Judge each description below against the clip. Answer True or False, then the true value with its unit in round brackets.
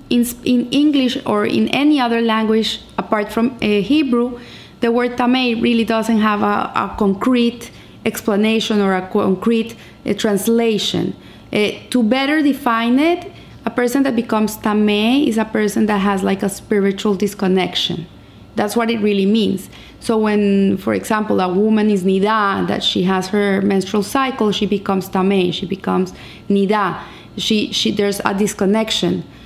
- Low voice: False (215 Hz)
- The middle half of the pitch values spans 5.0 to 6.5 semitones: False (2.7 semitones)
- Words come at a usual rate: True (155 wpm)